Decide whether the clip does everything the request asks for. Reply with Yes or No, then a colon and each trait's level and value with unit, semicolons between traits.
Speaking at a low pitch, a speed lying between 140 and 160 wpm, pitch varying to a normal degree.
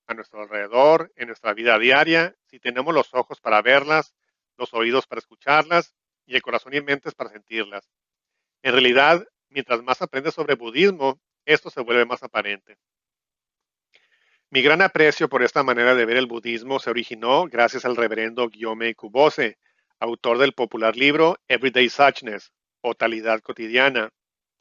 Yes: low, 125 Hz; average, 150 wpm; average, 3.6 semitones